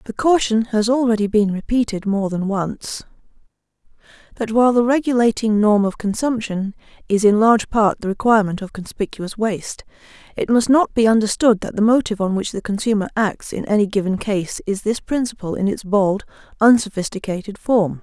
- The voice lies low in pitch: No, high, 215 Hz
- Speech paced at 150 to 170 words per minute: Yes, average, 165 wpm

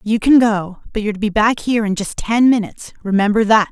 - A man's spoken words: No, female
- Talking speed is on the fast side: Yes, fast, 240 wpm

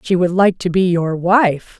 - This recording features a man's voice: No, female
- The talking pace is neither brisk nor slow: No, fast, 235 wpm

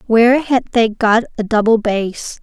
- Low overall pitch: No, high, 225 Hz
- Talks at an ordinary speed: Yes, average, 175 wpm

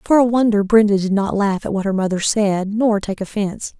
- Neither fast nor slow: No, fast, 235 wpm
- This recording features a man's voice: No, female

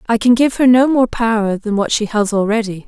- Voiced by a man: No, female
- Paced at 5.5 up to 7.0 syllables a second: Yes, 5.6 syllables/s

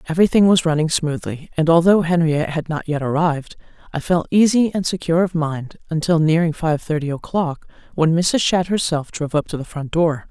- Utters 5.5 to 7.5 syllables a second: Yes, 5.6 syllables/s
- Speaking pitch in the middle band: Yes, medium, 160 Hz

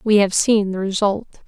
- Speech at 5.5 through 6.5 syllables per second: No, 5.0 syllables/s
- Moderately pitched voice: No, high, 205 Hz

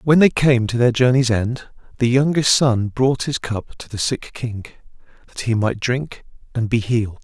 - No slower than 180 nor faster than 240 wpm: Yes, average, 200 wpm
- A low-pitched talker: Yes, low, 120 Hz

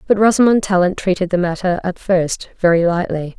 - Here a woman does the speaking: Yes, female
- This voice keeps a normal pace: Yes, average, 175 wpm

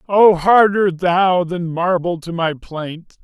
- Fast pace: No, average, 150 wpm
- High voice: No, medium, 180 Hz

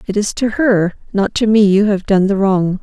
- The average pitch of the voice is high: Yes, high, 200 Hz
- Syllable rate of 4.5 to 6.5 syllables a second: Yes, 4.8 syllables/s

